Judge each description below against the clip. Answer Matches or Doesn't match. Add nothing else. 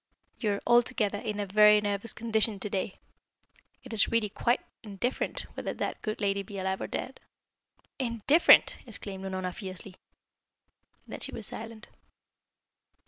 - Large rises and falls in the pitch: Doesn't match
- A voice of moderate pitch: Doesn't match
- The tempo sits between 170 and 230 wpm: Doesn't match